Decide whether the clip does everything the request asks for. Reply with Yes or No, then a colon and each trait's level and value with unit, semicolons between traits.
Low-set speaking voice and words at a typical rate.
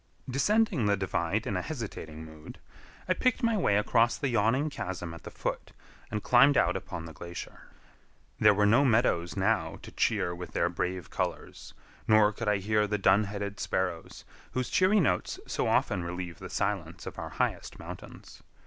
Yes: low, 105 Hz; average, 175 wpm